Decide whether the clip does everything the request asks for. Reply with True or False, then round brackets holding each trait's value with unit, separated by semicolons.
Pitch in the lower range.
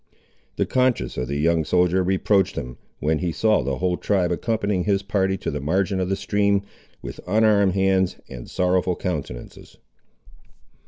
True (95 Hz)